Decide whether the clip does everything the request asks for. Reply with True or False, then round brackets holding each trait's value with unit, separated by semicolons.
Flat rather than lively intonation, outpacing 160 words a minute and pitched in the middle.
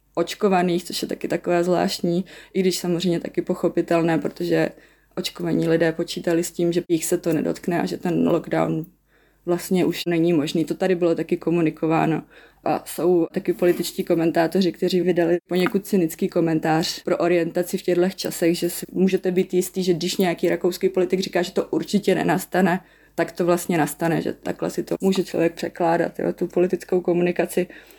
True (1.4 semitones; 170 wpm; 175 Hz)